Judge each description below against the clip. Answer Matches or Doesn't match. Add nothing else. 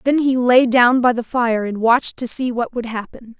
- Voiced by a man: Doesn't match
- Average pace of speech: Doesn't match